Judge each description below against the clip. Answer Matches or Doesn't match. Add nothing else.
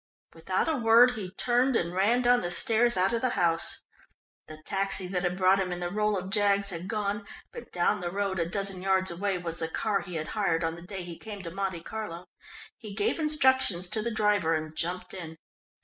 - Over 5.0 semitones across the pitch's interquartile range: Doesn't match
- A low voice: Doesn't match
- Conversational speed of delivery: Doesn't match